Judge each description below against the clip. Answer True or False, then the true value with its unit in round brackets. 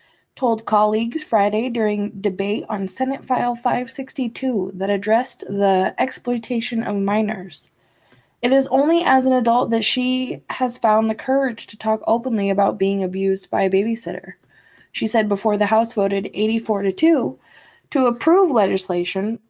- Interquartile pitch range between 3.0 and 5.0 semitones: True (3.7 semitones)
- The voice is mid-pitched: False (220 Hz)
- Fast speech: False (150 wpm)